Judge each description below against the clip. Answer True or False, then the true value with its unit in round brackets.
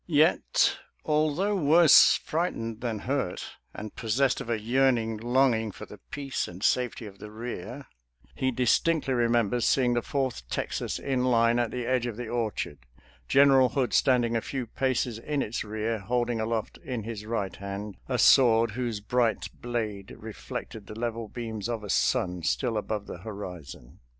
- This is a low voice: True (115 Hz)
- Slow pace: False (165 wpm)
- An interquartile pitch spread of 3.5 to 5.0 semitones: False (3.0 semitones)